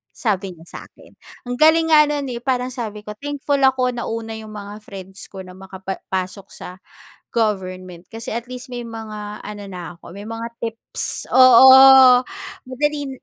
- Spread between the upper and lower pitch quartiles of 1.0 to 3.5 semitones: No, average, 4.7 semitones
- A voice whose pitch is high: Yes, high, 225 Hz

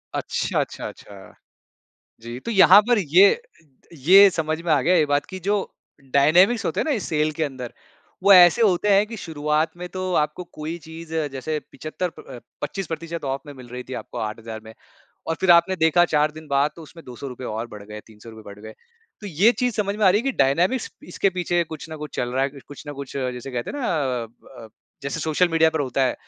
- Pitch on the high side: No, medium, 155 Hz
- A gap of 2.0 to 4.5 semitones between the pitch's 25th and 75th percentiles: No, average, 5.3 semitones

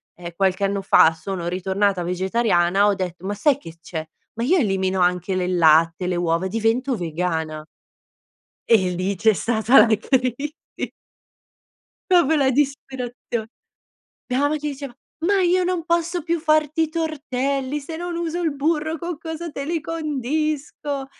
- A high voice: Yes, very high, 250 Hz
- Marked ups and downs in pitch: Yes, wide, 8.6 semitones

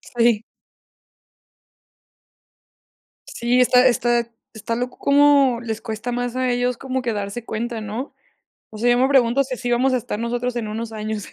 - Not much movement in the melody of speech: Yes, narrow, 1.9 semitones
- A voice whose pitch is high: Yes, high, 240 Hz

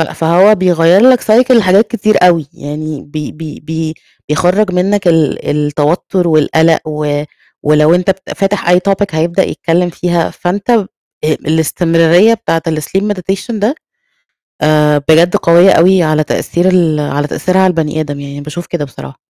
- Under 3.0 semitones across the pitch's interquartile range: No, average, 3.5 semitones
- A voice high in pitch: No, medium, 170 Hz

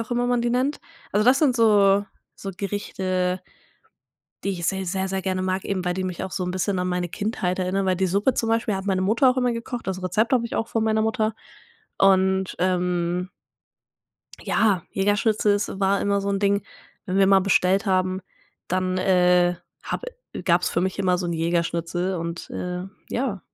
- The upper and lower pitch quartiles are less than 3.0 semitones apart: Yes, narrow, 2.5 semitones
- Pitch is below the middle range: No, high, 190 Hz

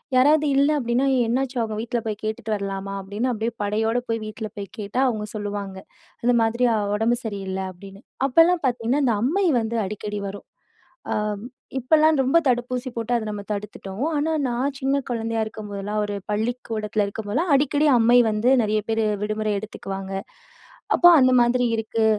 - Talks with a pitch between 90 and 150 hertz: No, high, 225 Hz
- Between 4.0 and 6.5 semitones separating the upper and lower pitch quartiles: No, average, 3.3 semitones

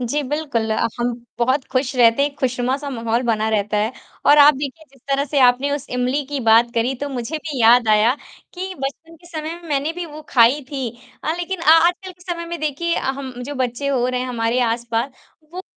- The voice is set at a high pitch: Yes, very high, 270 Hz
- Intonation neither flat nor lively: Yes, average, 3.8 semitones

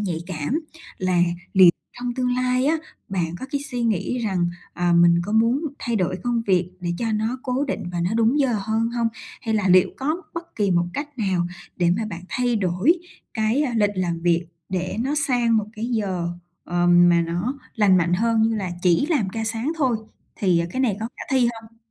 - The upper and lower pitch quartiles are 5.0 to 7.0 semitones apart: Yes, wide, 5.6 semitones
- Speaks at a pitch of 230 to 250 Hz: No, high, 220 Hz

